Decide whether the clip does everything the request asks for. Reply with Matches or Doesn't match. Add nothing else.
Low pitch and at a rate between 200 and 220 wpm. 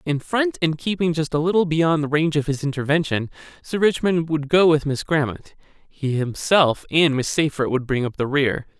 Doesn't match